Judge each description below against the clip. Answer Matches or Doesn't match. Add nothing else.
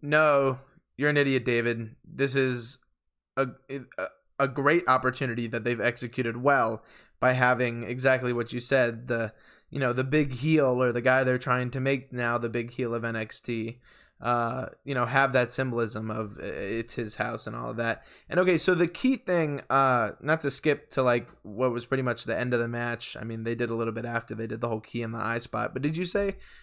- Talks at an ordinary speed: Doesn't match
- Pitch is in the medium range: Doesn't match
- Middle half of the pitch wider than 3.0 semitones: Doesn't match